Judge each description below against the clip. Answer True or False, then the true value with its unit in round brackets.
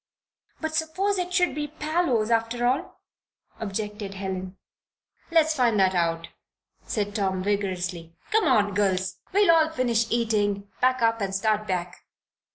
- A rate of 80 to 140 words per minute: True (135 wpm)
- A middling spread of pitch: False (7.4 semitones)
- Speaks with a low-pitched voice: False (220 Hz)